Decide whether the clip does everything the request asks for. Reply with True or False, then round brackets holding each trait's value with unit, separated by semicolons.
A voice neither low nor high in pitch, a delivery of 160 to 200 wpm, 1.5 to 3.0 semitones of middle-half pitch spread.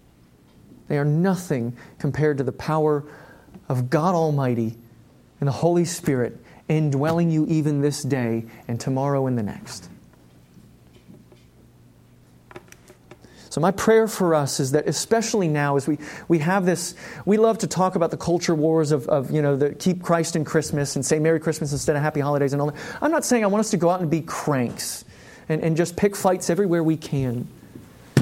False (150 Hz; 185 wpm; 4.0 semitones)